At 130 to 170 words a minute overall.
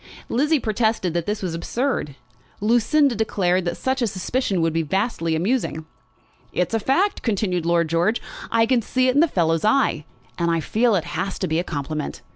No: average, 185 wpm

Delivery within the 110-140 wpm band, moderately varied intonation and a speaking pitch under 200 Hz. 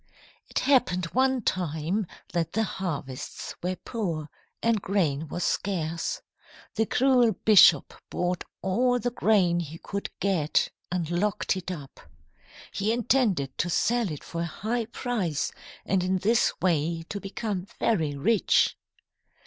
Yes: slow, 135 wpm; average, 4.9 semitones; medium, 185 Hz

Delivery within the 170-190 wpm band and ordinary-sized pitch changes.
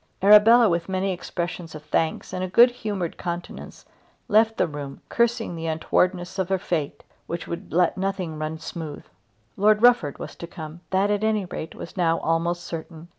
Yes: average, 175 wpm; average, 3.6 semitones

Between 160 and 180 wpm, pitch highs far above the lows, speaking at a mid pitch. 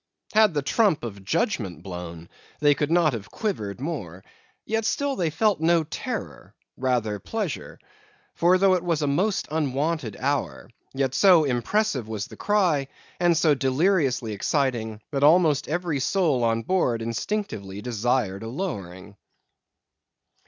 No: average, 140 wpm; wide, 7.5 semitones; medium, 145 Hz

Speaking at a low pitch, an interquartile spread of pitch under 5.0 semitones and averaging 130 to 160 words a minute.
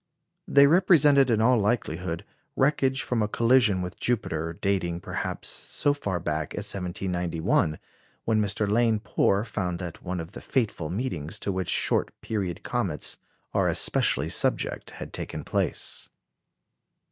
No: low, 100 Hz; wide, 5.5 semitones; average, 140 wpm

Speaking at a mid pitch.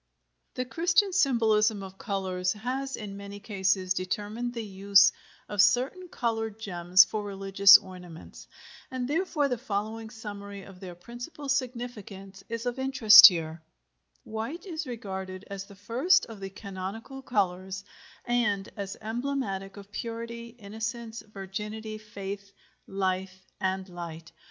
No: high, 210 Hz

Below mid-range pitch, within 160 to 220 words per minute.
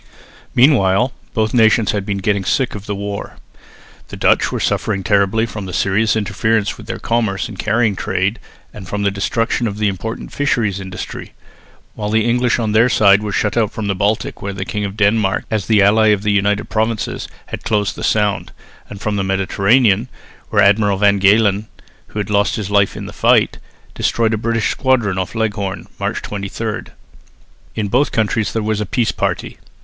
Yes: low, 105 Hz; average, 185 wpm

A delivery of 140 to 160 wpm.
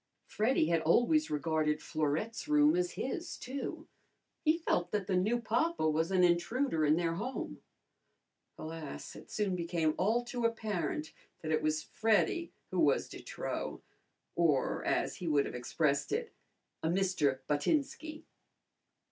Yes: average, 145 wpm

